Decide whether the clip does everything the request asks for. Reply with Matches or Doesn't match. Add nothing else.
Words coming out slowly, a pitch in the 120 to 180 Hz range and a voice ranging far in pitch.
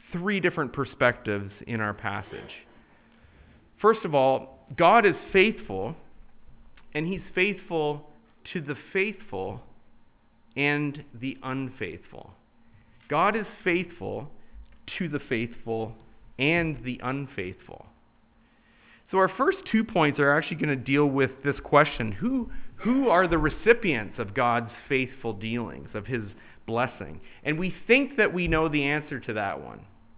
Matches